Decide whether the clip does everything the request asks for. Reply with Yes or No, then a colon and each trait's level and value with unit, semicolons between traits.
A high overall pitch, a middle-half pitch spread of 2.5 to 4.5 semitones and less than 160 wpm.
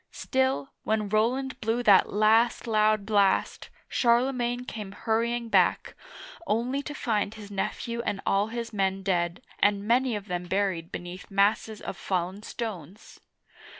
Yes: high, 215 Hz; average, 3.1 semitones; average, 140 wpm